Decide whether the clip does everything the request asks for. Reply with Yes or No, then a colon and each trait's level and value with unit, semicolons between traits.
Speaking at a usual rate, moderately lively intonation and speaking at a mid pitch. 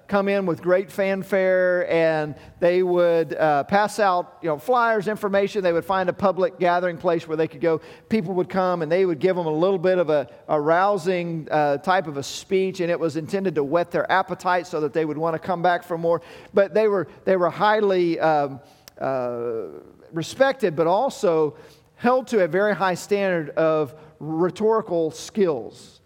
Yes: average, 195 wpm; average, 3.3 semitones; medium, 175 Hz